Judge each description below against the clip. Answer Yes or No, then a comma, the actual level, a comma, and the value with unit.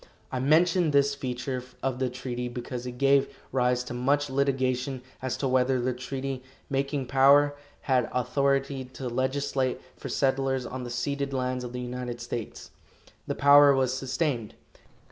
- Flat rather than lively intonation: Yes, narrow, 1.7 semitones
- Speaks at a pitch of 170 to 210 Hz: No, low, 130 Hz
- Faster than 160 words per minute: No, average, 155 wpm